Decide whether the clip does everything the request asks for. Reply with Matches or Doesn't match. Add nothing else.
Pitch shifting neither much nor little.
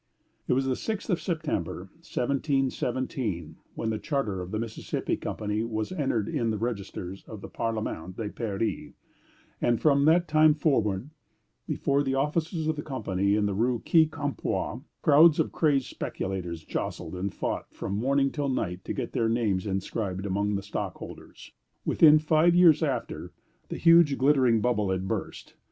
Doesn't match